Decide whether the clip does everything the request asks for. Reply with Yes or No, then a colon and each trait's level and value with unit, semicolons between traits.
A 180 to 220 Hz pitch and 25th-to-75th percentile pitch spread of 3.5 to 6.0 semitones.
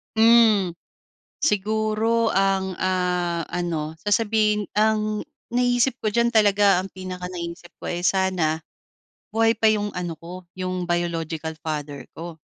Yes: high, 190 Hz; average, 3.8 semitones